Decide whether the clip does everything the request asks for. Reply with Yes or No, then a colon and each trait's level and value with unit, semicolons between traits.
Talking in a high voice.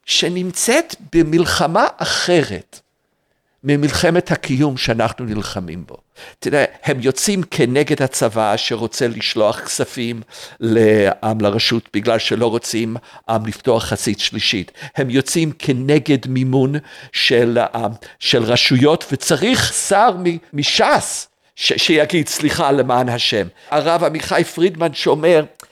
No: low, 135 Hz